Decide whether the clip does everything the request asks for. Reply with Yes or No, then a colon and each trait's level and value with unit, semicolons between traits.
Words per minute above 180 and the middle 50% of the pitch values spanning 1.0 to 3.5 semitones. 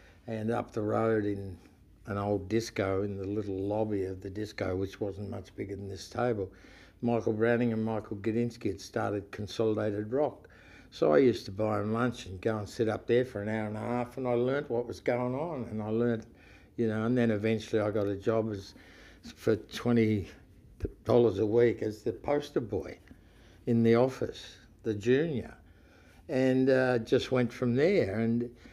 Yes: average, 190 wpm; average, 2.9 semitones